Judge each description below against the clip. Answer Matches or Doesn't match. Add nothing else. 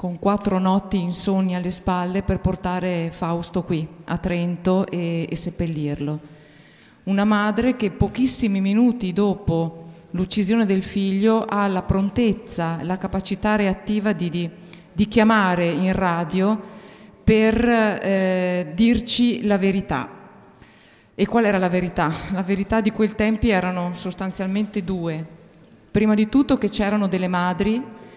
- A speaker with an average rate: Matches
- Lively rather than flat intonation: Doesn't match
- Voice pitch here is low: Doesn't match